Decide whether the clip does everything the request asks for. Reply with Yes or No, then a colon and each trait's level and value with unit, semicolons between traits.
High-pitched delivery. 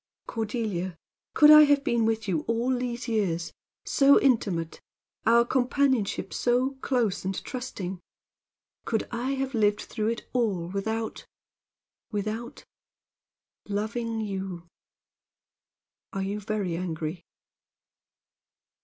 Yes: high, 220 Hz